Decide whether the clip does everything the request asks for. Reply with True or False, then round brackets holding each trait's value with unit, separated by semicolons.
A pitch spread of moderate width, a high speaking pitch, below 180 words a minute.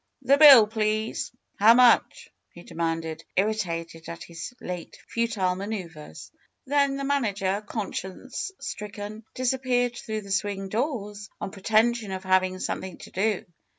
True (4.0 semitones; 210 Hz; 140 wpm)